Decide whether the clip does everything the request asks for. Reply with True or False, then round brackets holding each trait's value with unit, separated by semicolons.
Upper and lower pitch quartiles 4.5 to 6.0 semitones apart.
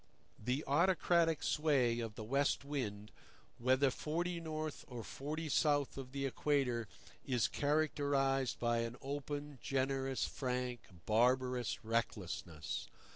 False (3.3 semitones)